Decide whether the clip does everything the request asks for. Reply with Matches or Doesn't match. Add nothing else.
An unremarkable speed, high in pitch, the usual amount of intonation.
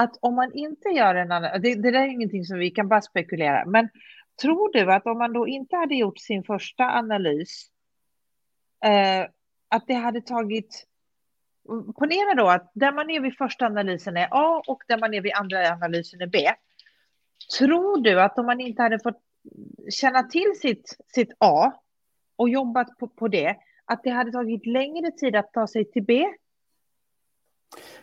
Matches